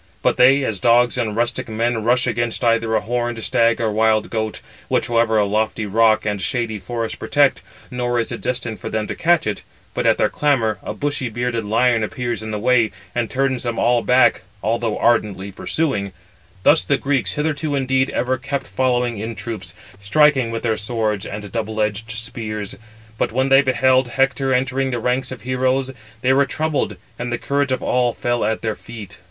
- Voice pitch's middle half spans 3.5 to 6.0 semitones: No, average, 2.8 semitones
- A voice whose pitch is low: Yes, low, 120 Hz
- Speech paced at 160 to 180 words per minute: No, average, 190 wpm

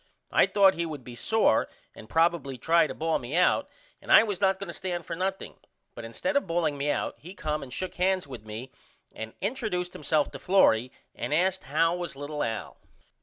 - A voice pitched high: No, medium, 165 Hz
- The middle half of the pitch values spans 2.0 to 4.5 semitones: No, average, 5.2 semitones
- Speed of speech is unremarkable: No, fast, 210 wpm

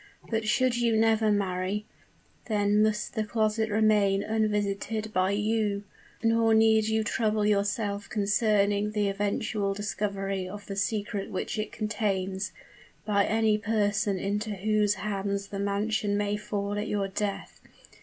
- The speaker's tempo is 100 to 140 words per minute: Yes, slow, 135 wpm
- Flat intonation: Yes, narrow, 1.3 semitones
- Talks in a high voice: Yes, high, 210 Hz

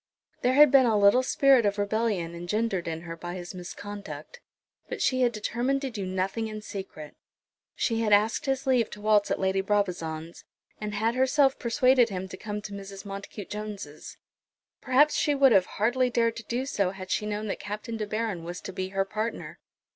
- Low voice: No, high, 210 Hz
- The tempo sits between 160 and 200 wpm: Yes, average, 195 wpm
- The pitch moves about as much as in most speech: Yes, average, 3.6 semitones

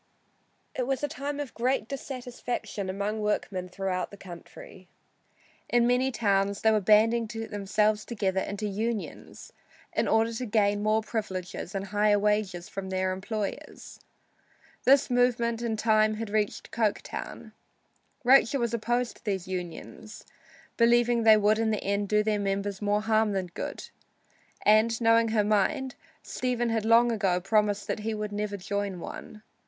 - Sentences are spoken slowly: No, average, 155 wpm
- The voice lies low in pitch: No, high, 215 Hz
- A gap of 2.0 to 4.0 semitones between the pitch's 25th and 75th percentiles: Yes, narrow, 2.4 semitones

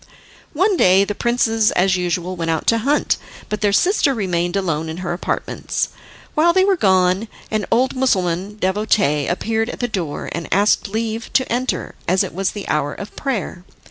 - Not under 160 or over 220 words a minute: Yes, average, 180 wpm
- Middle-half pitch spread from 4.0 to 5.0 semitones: Yes, average, 4.4 semitones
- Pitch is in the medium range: No, high, 200 Hz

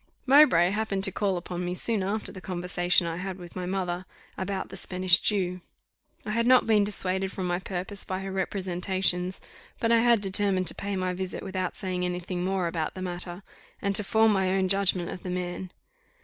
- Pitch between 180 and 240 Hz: Yes, medium, 185 Hz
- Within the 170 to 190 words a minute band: No, fast, 205 wpm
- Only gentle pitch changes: Yes, narrow, 1.7 semitones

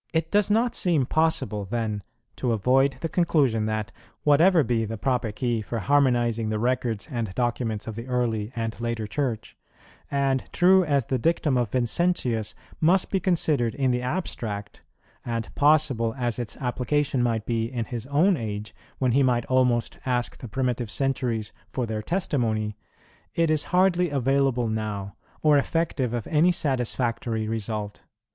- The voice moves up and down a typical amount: Yes, average, 4.3 semitones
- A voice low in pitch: Yes, low, 125 Hz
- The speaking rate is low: No, average, 155 wpm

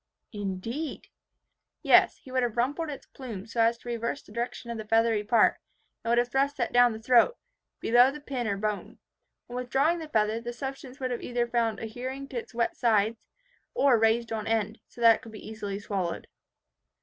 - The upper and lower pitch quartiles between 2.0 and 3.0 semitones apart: Yes, narrow, 2.5 semitones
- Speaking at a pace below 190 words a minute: No, average, 200 wpm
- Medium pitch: No, high, 235 Hz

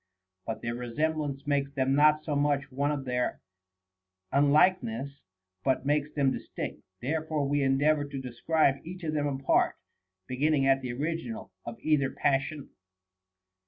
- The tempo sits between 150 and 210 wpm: No, average, 140 wpm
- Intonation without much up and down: Yes, narrow, 2.2 semitones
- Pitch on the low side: No, medium, 145 Hz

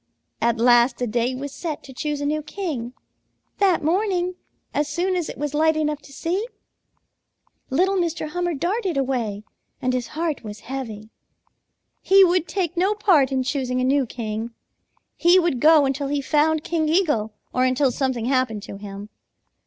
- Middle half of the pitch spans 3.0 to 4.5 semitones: No, average, 5.3 semitones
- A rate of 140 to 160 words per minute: No, average, 170 wpm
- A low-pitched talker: No, very high, 285 Hz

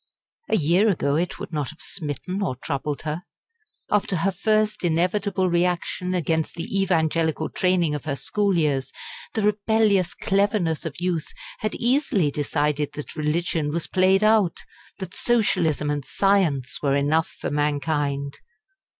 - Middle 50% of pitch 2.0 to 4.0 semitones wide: No, average, 4.6 semitones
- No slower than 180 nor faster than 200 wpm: No, average, 140 wpm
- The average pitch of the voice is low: No, medium, 170 Hz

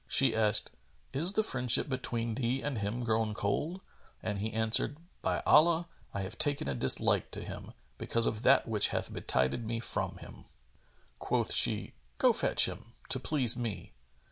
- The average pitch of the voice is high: No, low, 115 Hz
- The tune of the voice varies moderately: Yes, average, 4.0 semitones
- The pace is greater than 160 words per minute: Yes, average, 170 wpm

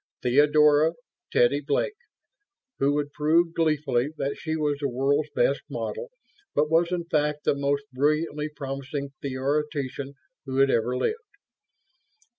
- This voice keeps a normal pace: No, slow, 130 wpm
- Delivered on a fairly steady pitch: Yes, narrow, 1.9 semitones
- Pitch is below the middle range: No, medium, 145 Hz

